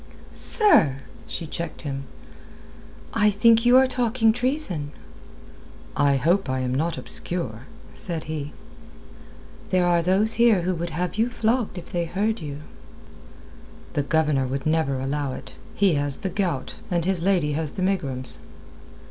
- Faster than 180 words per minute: No, average, 150 wpm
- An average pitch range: No, wide, 5.9 semitones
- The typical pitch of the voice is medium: Yes, medium, 170 Hz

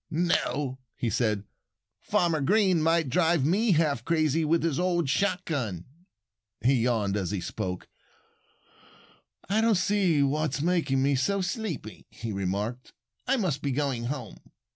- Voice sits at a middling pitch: Yes, medium, 150 Hz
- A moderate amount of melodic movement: No, wide, 6.0 semitones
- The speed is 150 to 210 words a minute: No, average, 140 wpm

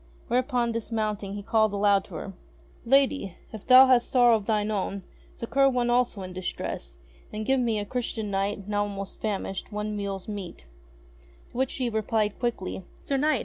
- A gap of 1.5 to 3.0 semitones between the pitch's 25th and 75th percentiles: No, average, 3.4 semitones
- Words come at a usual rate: Yes, average, 175 wpm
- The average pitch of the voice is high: Yes, high, 215 Hz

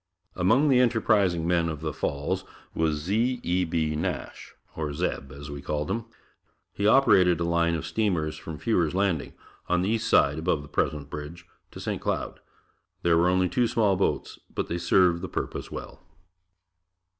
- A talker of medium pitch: No, very low, 85 Hz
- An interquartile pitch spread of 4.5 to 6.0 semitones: No, average, 4.0 semitones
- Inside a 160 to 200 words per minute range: Yes, average, 175 wpm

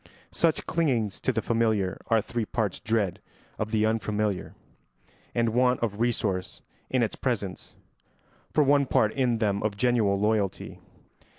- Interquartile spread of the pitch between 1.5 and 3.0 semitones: Yes, narrow, 2.6 semitones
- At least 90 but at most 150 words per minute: Yes, average, 140 wpm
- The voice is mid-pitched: No, low, 110 Hz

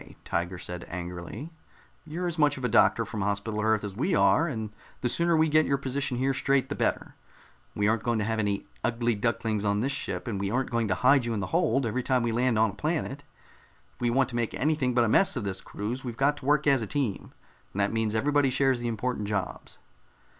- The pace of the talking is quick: Yes, fast, 240 wpm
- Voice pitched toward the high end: No, low, 120 Hz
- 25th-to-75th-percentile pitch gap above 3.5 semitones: Yes, average, 4.4 semitones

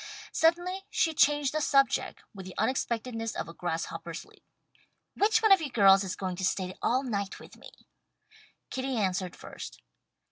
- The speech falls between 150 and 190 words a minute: Yes, average, 165 wpm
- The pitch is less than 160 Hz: No, high, 240 Hz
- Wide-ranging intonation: Yes, wide, 7.5 semitones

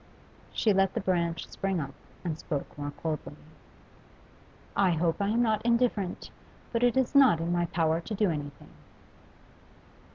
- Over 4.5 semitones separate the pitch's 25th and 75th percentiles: Yes, average, 4.9 semitones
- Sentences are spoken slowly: No, average, 155 wpm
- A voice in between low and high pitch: Yes, medium, 180 Hz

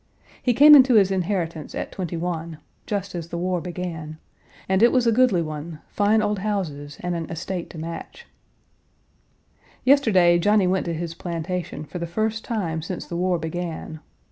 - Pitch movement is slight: No, average, 3.8 semitones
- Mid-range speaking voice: Yes, medium, 180 Hz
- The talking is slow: No, average, 170 wpm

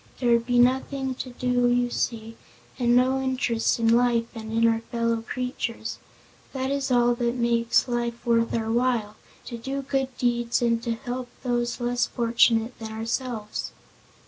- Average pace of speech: Yes, average, 165 wpm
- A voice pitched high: Yes, high, 240 Hz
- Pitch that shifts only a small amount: Yes, narrow, 1.4 semitones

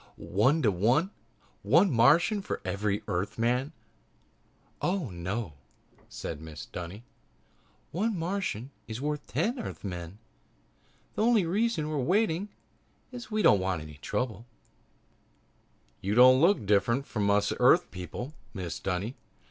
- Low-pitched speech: Yes, low, 120 Hz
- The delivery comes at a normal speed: No, slow, 125 wpm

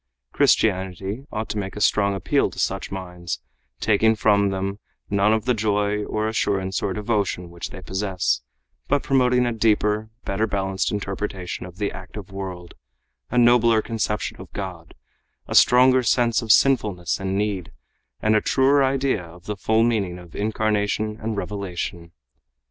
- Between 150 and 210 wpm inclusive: Yes, average, 155 wpm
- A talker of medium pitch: No, low, 105 Hz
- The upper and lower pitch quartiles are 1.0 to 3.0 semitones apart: Yes, average, 2.7 semitones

